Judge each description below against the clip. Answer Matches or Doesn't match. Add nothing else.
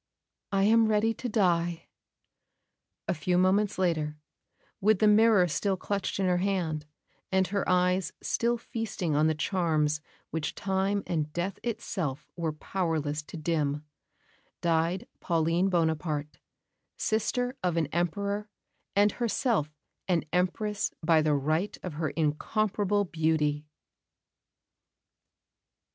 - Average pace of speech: Doesn't match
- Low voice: Doesn't match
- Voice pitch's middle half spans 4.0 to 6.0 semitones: Matches